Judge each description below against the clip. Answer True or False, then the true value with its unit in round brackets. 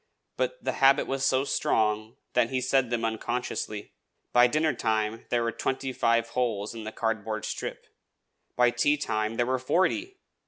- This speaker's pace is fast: False (160 wpm)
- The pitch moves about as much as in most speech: True (3.1 semitones)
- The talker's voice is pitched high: False (120 Hz)